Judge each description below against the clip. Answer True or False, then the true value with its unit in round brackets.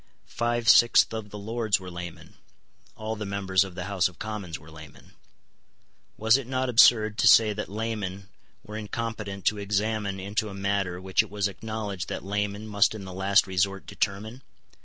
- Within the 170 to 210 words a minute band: True (180 wpm)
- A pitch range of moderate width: False (2.2 semitones)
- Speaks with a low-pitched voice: True (100 Hz)